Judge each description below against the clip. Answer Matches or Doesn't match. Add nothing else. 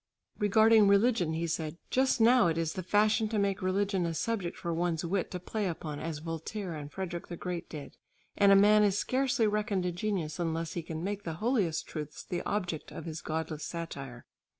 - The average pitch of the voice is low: Doesn't match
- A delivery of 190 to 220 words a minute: Matches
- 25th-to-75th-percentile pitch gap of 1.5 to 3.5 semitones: Doesn't match